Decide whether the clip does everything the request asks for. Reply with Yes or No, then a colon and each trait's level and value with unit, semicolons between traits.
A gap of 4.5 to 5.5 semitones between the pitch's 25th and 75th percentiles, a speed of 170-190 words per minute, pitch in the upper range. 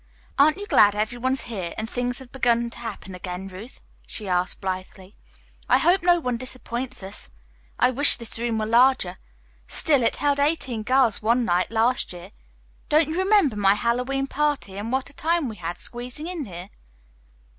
Yes: average, 4.9 semitones; average, 180 wpm; high, 240 Hz